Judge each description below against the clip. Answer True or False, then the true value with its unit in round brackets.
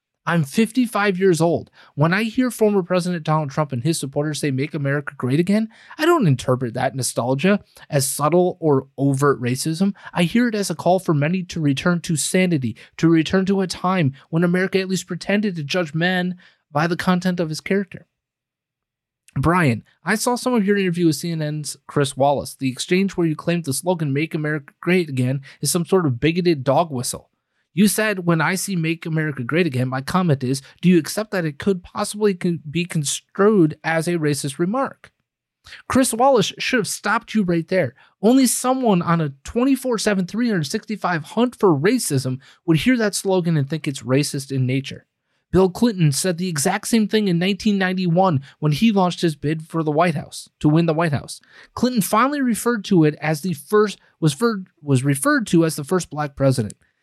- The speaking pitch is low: False (170 Hz)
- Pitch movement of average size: True (4.7 semitones)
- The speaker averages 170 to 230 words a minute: True (195 wpm)